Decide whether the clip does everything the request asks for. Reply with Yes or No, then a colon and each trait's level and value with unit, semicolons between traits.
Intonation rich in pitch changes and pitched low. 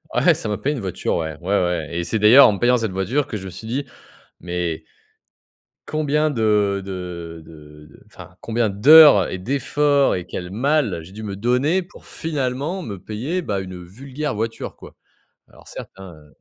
Yes: wide, 7.3 semitones; low, 105 Hz